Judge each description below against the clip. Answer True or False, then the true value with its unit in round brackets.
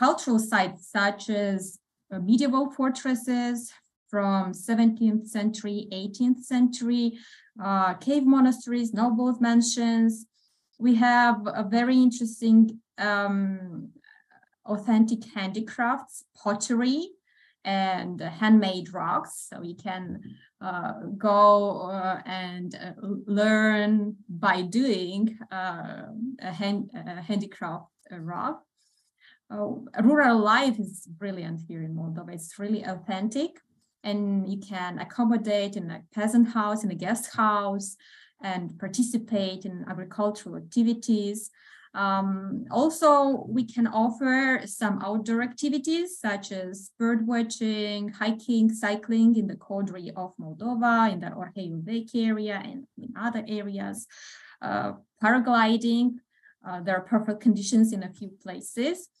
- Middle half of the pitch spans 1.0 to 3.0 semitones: False (3.4 semitones)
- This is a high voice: True (215 Hz)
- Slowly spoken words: True (115 wpm)